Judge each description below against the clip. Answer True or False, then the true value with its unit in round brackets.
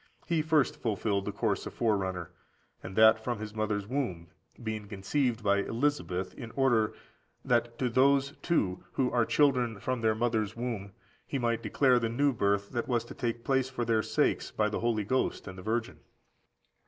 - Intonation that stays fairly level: False (3.4 semitones)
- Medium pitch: False (115 Hz)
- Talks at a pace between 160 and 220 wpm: True (180 wpm)